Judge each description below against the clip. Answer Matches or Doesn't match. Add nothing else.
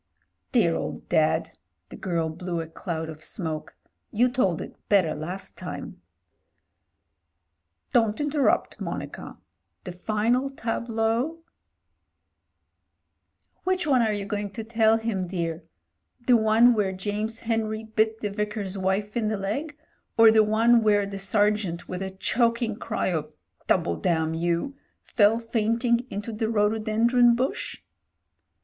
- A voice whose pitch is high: Matches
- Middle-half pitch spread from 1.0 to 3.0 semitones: Doesn't match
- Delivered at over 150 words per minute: Doesn't match